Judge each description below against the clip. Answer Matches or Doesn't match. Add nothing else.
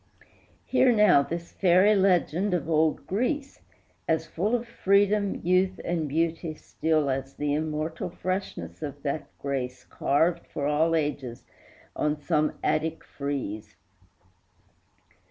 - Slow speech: Matches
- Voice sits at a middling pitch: Matches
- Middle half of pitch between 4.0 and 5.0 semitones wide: Matches